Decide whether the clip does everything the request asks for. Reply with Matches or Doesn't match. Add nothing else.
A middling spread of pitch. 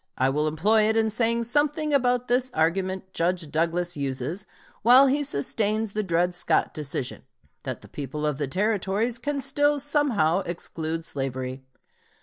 Doesn't match